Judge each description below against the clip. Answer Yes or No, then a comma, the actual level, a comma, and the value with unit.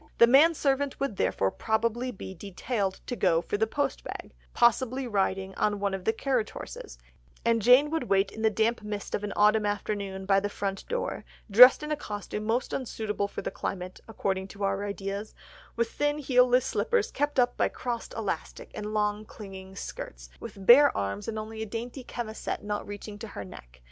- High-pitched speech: Yes, high, 215 Hz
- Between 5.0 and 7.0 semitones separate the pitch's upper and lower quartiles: No, average, 3.8 semitones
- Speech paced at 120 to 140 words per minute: No, average, 195 wpm